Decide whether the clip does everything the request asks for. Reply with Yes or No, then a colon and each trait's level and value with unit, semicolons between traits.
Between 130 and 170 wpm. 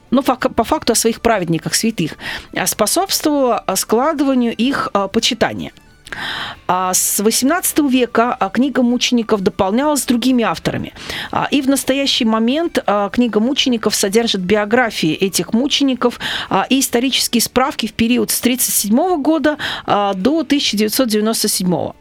No: slow, 110 wpm